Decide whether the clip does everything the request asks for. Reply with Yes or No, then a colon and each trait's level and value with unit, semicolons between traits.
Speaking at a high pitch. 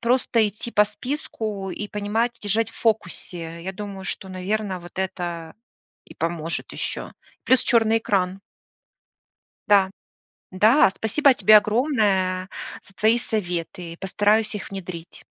Yes: high, 205 Hz